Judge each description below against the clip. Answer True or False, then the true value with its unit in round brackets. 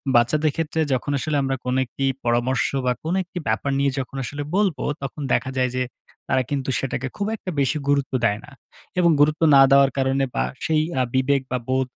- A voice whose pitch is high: False (135 Hz)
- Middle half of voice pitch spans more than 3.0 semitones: False (2.7 semitones)